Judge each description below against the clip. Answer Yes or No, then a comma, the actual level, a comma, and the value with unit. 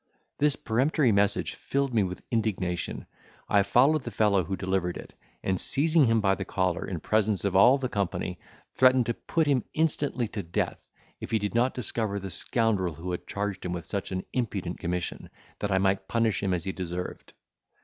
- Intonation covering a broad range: No, average, 4.3 semitones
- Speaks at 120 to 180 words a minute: No, average, 190 wpm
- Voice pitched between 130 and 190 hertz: No, low, 100 Hz